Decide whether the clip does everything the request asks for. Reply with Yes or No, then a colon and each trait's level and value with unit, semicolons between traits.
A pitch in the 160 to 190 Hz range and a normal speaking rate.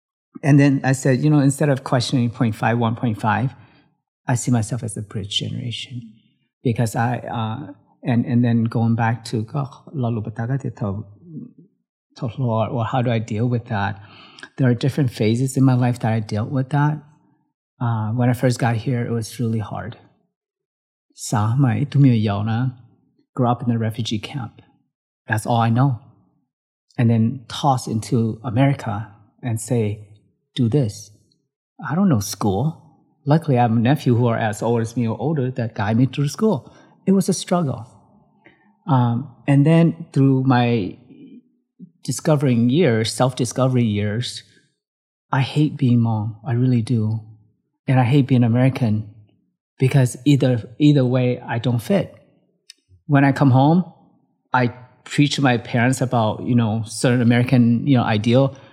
No: low, 125 Hz; average, 150 wpm